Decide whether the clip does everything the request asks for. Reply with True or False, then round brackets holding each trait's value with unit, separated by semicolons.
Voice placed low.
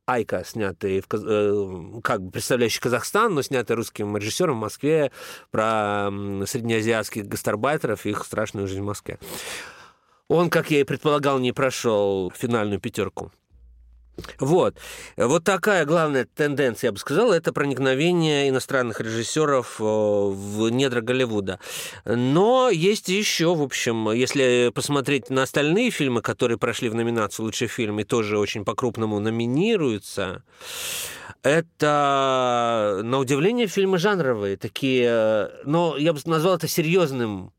True (125 Hz)